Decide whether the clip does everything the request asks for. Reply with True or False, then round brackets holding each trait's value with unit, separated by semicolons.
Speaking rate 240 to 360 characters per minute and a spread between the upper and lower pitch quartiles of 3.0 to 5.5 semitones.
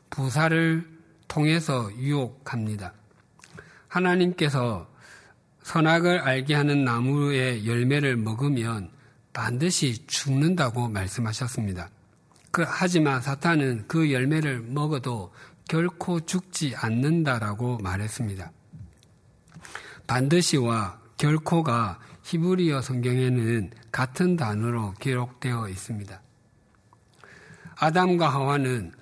False (220 characters per minute; 5.2 semitones)